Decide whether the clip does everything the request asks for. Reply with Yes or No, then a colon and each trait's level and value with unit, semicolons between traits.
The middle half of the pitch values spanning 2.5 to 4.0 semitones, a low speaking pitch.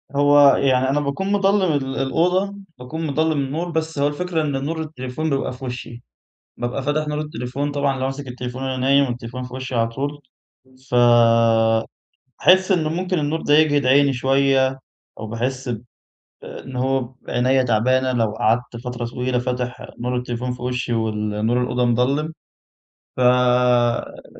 Yes: average, 2.9 semitones; low, 130 Hz